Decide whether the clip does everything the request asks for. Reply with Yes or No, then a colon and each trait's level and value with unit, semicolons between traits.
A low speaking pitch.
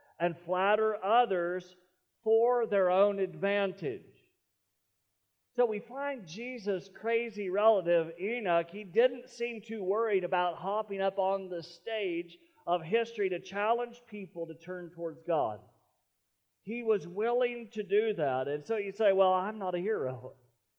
No: high, 195 Hz